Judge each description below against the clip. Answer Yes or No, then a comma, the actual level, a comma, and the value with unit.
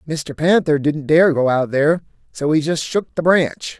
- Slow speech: No, fast, 205 wpm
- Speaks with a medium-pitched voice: Yes, medium, 150 Hz